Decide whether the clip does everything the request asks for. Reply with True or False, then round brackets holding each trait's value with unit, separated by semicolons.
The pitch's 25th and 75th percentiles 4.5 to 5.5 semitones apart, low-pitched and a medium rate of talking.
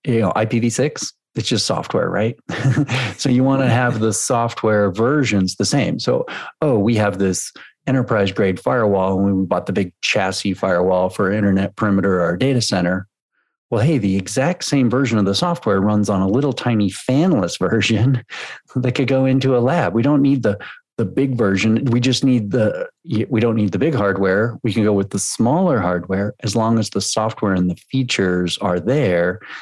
True (4.8 semitones; 110 Hz; 190 wpm)